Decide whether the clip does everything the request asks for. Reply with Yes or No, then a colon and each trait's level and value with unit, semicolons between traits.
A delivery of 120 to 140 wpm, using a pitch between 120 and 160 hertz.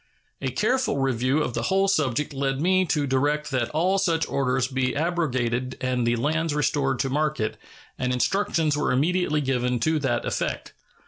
No: average, 170 wpm; medium, 140 Hz